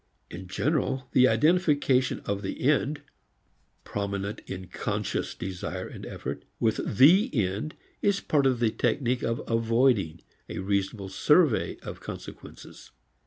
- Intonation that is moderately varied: No, wide, 6.0 semitones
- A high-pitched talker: No, low, 115 Hz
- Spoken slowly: Yes, slow, 125 wpm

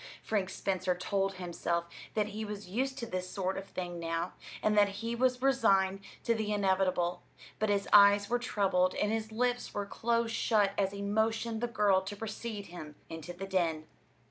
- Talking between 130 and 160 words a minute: No, average, 185 wpm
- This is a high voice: Yes, high, 200 Hz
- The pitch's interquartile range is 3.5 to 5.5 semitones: No, average, 3.0 semitones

